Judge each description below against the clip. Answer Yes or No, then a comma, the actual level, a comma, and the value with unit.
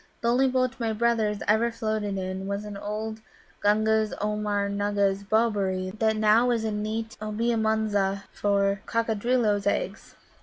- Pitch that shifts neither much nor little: No, narrow, 1.8 semitones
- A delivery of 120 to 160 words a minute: Yes, average, 150 wpm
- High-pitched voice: Yes, high, 215 Hz